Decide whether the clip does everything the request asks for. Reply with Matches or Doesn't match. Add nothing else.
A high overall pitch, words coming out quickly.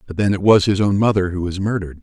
Doesn't match